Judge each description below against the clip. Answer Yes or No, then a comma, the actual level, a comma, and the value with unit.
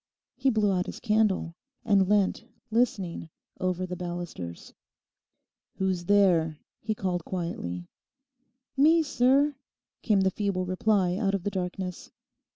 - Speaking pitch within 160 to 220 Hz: Yes, high, 190 Hz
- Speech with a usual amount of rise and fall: Yes, average, 3.1 semitones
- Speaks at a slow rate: Yes, slow, 125 wpm